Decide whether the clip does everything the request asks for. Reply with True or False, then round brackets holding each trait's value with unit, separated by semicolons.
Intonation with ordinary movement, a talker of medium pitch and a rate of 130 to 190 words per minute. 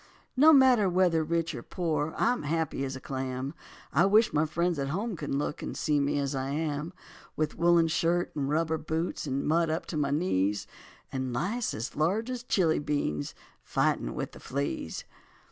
True (3.7 semitones; 155 Hz; 185 wpm)